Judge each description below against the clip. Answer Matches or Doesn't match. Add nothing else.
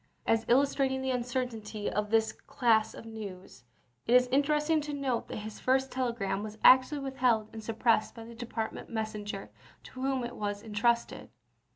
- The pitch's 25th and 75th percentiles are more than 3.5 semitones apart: Doesn't match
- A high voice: Matches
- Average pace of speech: Matches